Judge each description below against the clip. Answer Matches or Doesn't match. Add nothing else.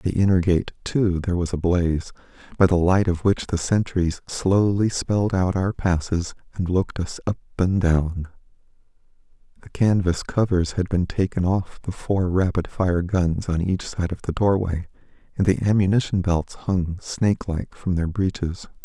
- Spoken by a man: Matches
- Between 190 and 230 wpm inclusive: Doesn't match